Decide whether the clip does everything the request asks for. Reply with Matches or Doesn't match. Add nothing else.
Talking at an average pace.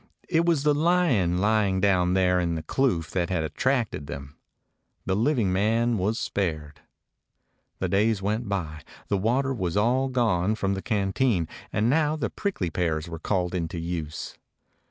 Matches